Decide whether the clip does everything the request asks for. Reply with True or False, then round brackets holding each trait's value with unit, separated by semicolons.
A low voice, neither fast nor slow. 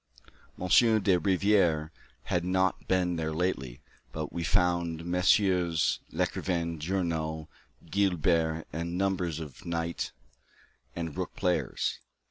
False (85 Hz; 105 wpm)